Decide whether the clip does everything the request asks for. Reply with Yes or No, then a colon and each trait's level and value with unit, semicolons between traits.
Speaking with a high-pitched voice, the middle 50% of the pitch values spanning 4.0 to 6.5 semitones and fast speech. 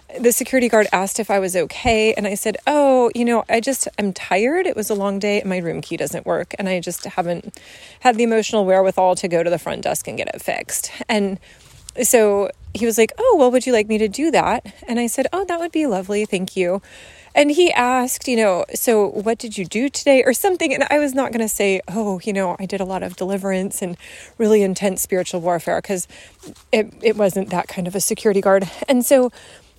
Yes: high, 215 Hz; average, 4.4 semitones; fast, 235 wpm